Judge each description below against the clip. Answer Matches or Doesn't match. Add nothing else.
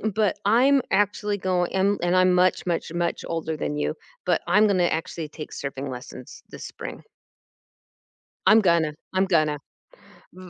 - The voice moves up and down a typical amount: Matches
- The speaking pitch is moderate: Matches